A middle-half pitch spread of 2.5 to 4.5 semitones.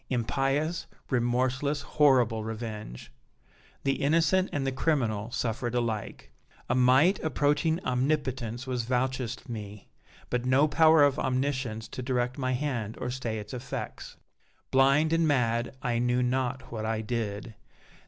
Yes: average, 3.0 semitones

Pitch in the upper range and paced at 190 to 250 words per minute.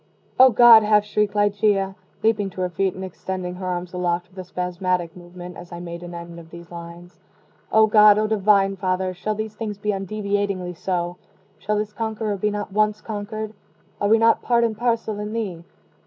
Yes: high, 200 Hz; average, 195 wpm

